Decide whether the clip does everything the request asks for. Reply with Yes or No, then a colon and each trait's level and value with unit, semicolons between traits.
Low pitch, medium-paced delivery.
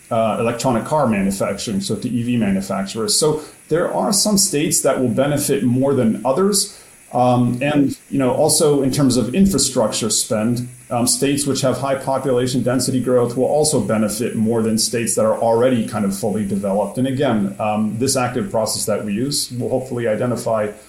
Yes: low, 125 Hz; average, 180 wpm